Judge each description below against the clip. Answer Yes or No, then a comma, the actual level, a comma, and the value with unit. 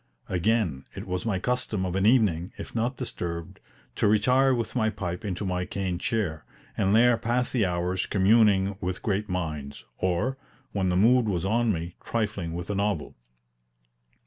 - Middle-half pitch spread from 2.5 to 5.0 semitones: Yes, average, 3.9 semitones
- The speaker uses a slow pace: No, average, 170 wpm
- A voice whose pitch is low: Yes, low, 100 Hz